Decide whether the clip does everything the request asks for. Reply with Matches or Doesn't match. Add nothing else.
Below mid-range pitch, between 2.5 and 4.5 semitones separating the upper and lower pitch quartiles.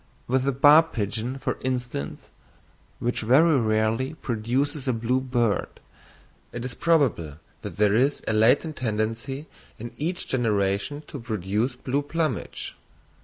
Matches